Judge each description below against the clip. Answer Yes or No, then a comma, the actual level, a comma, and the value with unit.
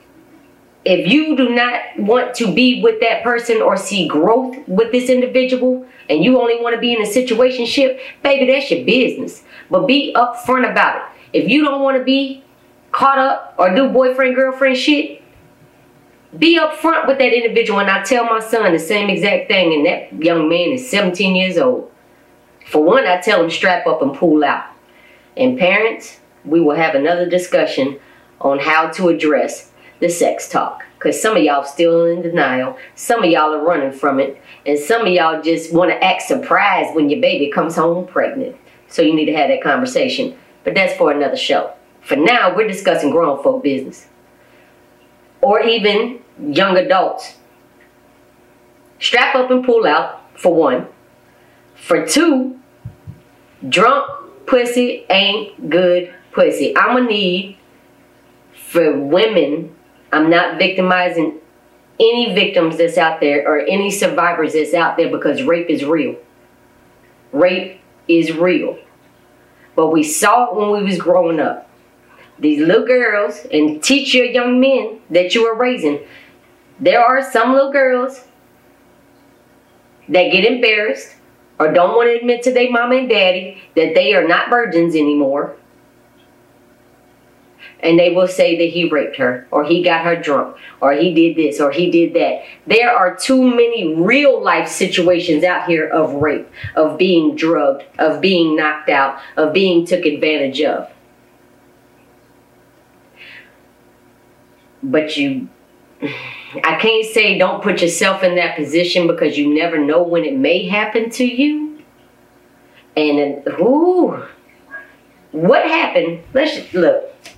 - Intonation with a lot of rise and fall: Yes, wide, 7.3 semitones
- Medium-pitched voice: No, high, 200 Hz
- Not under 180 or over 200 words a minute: No, average, 155 wpm